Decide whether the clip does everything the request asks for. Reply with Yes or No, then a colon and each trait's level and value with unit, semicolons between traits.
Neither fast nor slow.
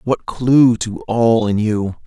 Yes: average, 175 wpm